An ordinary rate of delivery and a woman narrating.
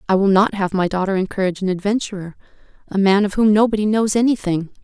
Yes: average, 185 wpm; female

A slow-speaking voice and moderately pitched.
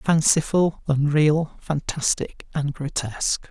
Yes: slow, 85 wpm; medium, 150 Hz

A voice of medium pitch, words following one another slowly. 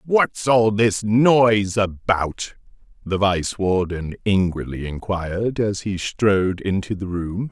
No: low, 100 Hz; slow, 130 wpm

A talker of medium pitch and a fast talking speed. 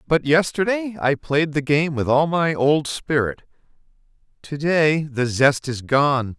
No: medium, 150 Hz; average, 160 wpm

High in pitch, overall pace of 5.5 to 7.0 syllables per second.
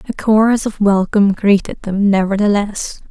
No: high, 205 Hz; 5.0 syllables/s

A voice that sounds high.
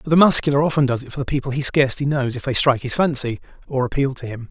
No: low, 135 Hz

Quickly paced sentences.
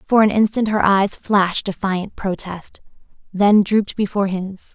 No: average, 150 wpm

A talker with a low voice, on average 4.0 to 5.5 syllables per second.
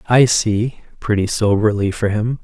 Yes: low, 110 Hz; 4.4 syllables/s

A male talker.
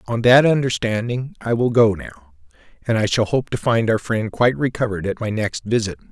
Yes: male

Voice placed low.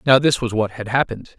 Yes: low, 120 Hz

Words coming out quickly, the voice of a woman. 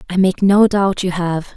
Yes: fast, 230 wpm; female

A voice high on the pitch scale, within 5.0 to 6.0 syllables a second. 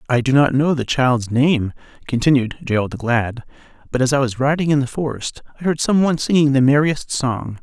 No: low, 135 Hz; 5.5 syllables/s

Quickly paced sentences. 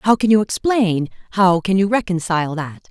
No: average, 165 wpm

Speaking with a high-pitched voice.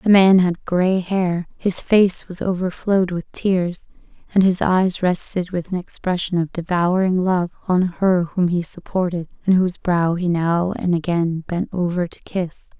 No: medium, 180 Hz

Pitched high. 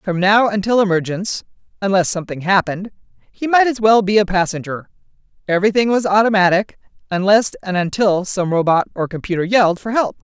Yes: high, 195 Hz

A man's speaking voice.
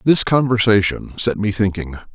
Yes: male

